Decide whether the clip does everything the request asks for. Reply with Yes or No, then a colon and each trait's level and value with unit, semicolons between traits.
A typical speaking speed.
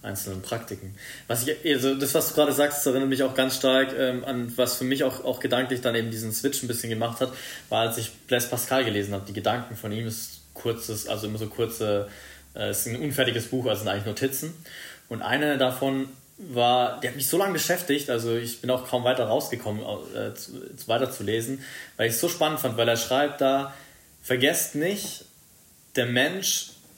No: fast, 205 wpm